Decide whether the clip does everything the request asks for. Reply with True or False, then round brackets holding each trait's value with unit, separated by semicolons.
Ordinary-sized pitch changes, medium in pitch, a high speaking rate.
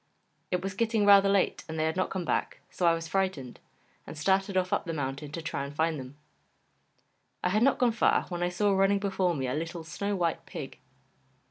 True (3.6 semitones; 180 Hz; 220 wpm)